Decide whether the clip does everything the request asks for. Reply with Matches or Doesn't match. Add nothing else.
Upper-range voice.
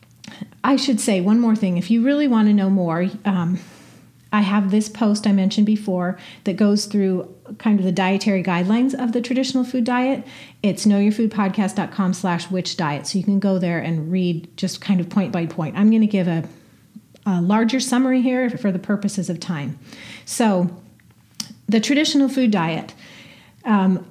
Matches